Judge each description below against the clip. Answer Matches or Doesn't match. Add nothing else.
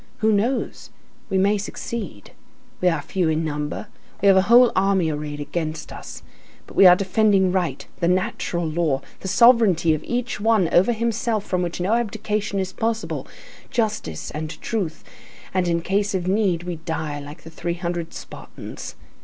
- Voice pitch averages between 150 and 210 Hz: Matches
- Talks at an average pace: Matches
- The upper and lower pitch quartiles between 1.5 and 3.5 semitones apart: Doesn't match